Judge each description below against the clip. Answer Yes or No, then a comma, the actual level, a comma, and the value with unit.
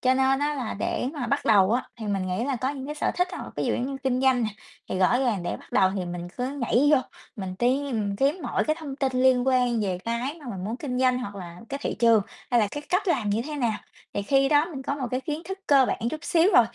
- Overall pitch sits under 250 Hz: No, very high, 255 Hz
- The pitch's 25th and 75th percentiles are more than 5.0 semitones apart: No, average, 4.3 semitones